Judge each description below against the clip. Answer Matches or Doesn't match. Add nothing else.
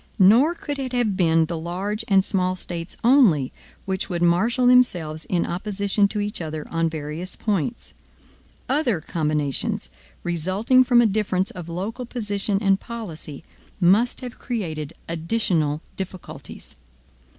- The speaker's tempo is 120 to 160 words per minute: Matches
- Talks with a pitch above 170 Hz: Matches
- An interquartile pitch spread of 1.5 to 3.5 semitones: Doesn't match